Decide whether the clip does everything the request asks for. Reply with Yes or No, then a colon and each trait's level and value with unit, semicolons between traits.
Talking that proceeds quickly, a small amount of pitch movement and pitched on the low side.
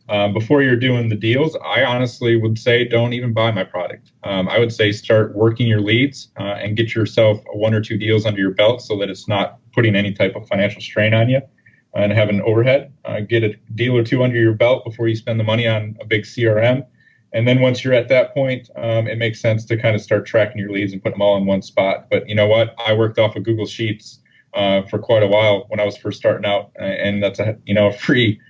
Yes: fast, 255 wpm; narrow, 2.1 semitones; low, 110 Hz